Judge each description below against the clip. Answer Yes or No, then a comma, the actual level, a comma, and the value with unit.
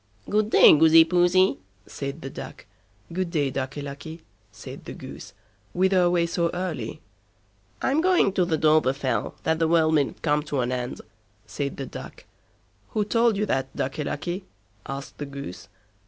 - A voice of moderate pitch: Yes, medium, 160 Hz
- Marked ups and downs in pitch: No, average, 4.5 semitones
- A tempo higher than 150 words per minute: Yes, average, 160 wpm